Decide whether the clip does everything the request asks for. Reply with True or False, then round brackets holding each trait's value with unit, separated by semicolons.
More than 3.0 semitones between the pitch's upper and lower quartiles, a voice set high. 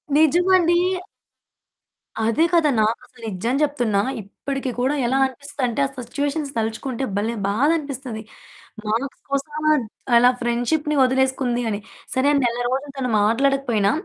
True (3.6 semitones; 260 Hz)